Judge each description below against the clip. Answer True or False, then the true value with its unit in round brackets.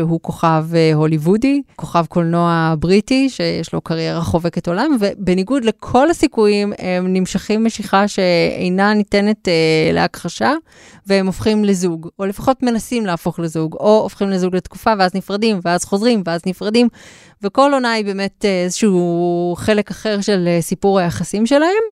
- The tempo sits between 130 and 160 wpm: True (140 wpm)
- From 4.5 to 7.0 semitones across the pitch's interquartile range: False (3.8 semitones)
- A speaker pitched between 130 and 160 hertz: False (195 Hz)